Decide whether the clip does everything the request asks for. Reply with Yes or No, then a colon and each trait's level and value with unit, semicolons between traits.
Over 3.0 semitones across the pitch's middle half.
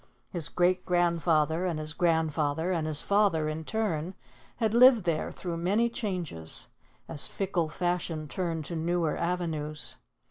No: average, 2.7 semitones